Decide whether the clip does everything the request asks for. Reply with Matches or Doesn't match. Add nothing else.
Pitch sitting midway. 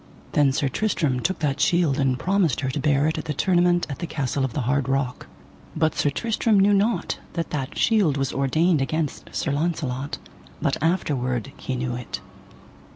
Matches